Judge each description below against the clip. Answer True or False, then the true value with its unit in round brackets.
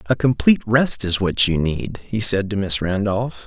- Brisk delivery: True (210 wpm)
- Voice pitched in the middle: False (100 Hz)